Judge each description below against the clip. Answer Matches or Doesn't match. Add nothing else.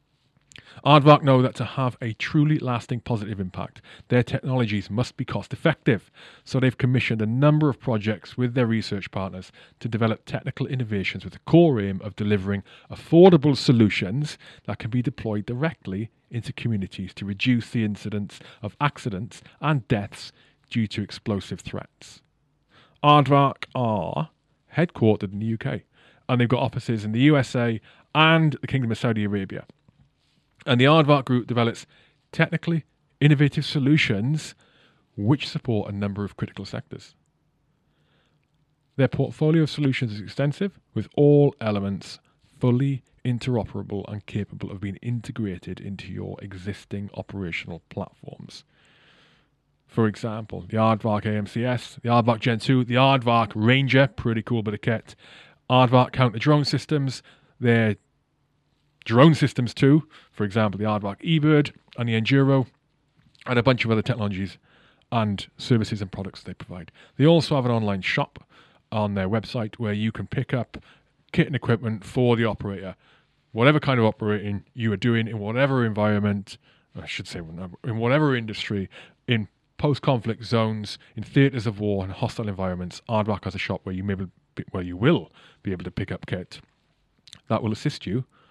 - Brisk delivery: Doesn't match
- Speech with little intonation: Doesn't match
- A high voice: Doesn't match